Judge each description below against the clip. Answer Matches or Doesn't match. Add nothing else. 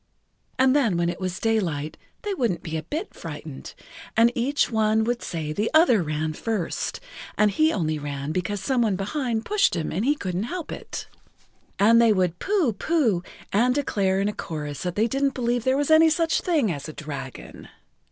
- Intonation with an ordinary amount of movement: Doesn't match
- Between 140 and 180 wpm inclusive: Doesn't match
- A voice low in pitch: Doesn't match